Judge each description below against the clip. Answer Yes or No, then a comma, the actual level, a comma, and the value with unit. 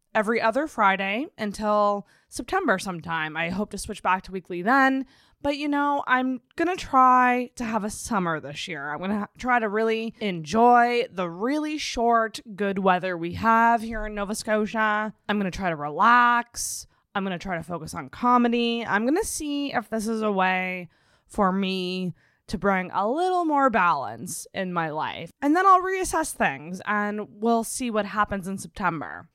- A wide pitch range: No, average, 4.4 semitones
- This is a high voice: Yes, high, 215 Hz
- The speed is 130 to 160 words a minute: No, average, 175 wpm